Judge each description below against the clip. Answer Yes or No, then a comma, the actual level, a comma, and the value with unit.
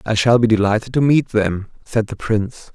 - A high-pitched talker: No, low, 110 Hz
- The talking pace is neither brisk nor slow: No, fast, 220 wpm